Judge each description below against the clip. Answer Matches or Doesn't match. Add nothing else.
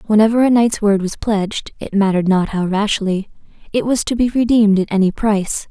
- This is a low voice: Doesn't match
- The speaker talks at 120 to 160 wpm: Doesn't match